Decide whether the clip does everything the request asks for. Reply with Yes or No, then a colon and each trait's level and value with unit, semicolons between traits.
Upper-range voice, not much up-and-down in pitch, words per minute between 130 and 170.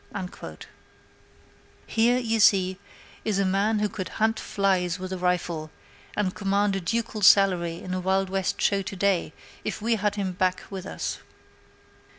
Yes: high, 195 Hz; narrow, 2.1 semitones; average, 160 wpm